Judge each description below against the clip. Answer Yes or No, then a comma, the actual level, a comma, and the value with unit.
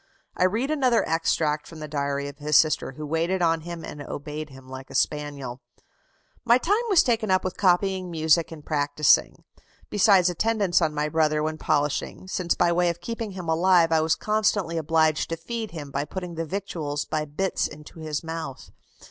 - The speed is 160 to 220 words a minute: Yes, average, 190 wpm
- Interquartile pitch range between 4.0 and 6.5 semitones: No, average, 3.6 semitones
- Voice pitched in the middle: Yes, medium, 165 Hz